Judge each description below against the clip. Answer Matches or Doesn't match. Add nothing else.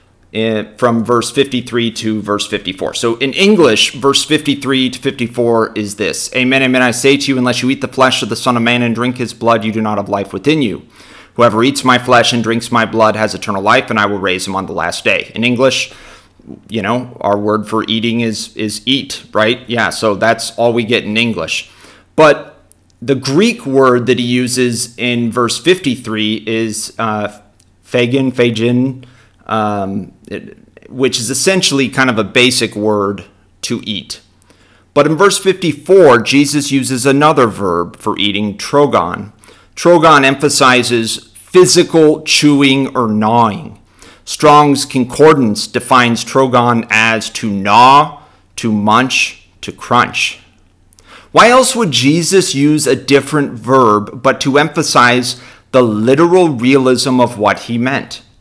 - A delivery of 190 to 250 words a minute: Doesn't match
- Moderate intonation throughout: Matches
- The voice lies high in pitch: Doesn't match